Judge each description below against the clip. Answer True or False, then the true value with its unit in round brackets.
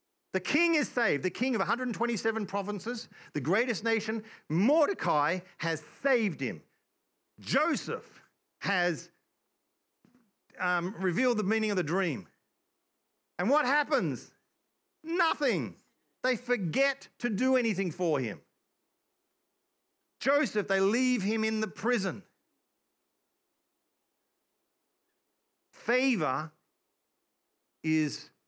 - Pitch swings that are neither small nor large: False (7.6 semitones)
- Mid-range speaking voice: False (230 Hz)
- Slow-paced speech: True (95 wpm)